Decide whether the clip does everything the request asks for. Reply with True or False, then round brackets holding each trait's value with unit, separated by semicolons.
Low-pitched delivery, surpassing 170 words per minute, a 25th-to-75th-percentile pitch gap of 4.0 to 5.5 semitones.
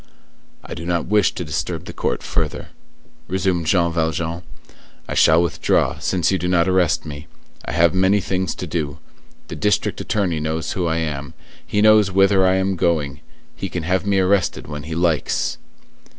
False (85 Hz; 180 wpm; 2.8 semitones)